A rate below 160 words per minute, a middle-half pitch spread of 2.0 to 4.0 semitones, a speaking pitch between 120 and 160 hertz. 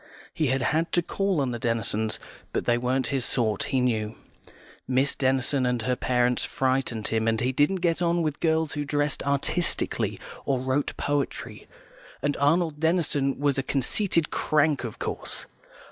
No: average, 165 wpm; average, 3.7 semitones; low, 135 Hz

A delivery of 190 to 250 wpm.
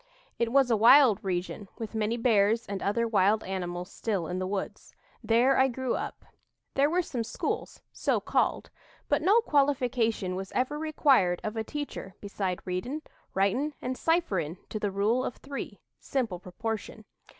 No: average, 160 wpm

